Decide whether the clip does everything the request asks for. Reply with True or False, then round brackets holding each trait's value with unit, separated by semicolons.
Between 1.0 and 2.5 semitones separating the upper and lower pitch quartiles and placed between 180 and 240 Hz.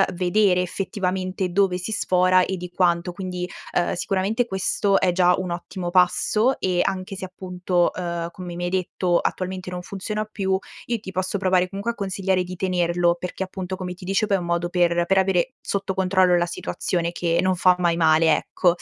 True (1.3 semitones; 185 Hz)